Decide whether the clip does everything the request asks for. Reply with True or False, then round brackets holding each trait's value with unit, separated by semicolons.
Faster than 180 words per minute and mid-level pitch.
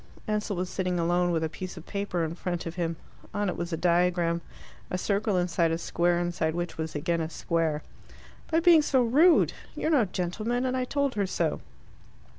True (200 wpm; 180 Hz)